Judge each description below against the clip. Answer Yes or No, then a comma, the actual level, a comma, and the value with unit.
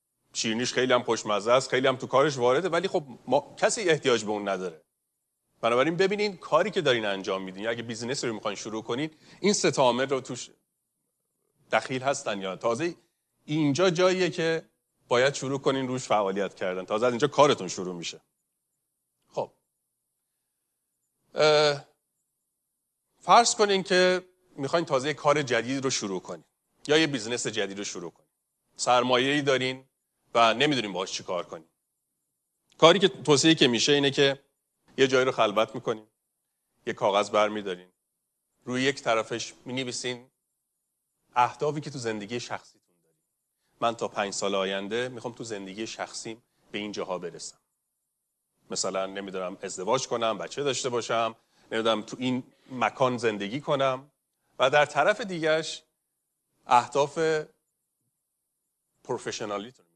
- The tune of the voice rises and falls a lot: No, average, 4.9 semitones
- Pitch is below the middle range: Yes, low, 125 Hz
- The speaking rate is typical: Yes, average, 140 wpm